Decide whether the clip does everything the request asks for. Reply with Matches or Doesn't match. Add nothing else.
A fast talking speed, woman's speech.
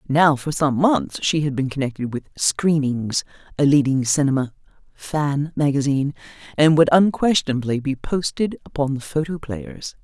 Doesn't match